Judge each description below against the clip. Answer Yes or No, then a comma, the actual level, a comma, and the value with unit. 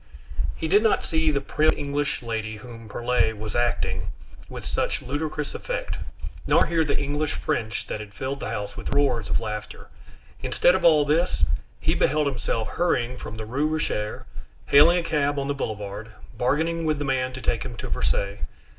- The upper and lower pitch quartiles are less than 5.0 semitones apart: No, wide, 5.4 semitones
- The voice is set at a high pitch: No, medium, 140 Hz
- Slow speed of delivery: No, average, 180 wpm